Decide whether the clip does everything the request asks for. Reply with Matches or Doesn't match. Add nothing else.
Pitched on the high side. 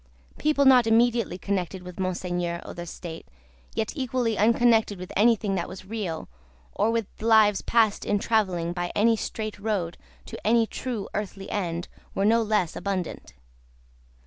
Matches